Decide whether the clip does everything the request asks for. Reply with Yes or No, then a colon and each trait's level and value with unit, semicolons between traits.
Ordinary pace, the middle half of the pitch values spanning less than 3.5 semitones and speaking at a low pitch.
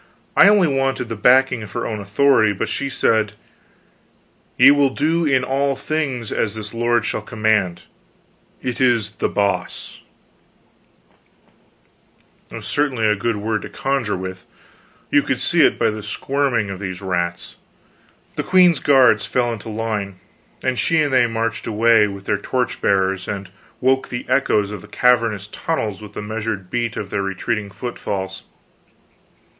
No: average, 160 wpm; average, 4.1 semitones; low, 110 Hz